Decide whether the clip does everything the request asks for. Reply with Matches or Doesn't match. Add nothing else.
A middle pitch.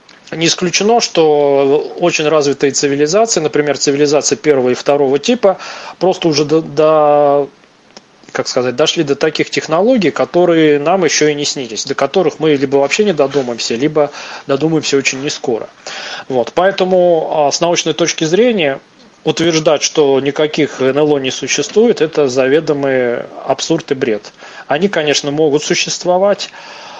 Matches